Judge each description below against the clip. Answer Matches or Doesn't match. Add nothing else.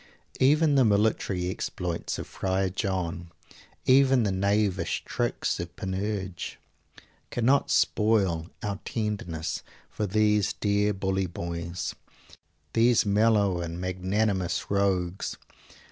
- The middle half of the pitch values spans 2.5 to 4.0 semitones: Matches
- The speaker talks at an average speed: Doesn't match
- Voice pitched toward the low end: Matches